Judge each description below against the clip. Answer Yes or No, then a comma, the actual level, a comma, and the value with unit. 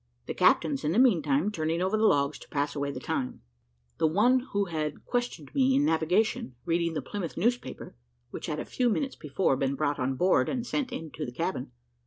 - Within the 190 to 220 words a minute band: Yes, fast, 205 wpm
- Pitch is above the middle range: No, medium, 165 Hz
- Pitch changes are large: Yes, wide, 7.3 semitones